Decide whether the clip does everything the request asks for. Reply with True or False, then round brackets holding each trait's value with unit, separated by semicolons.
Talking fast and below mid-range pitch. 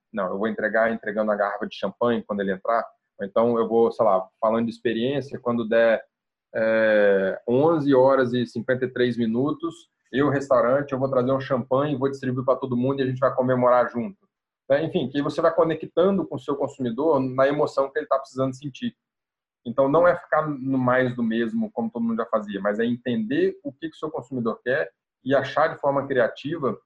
True (205 wpm; 130 Hz)